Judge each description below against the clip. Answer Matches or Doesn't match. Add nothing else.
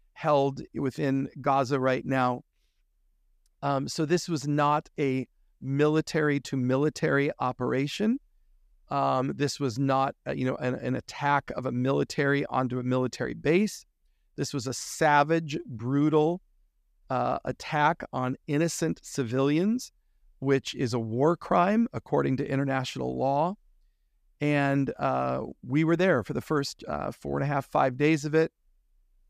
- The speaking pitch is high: Doesn't match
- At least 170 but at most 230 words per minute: Doesn't match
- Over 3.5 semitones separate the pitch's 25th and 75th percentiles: Doesn't match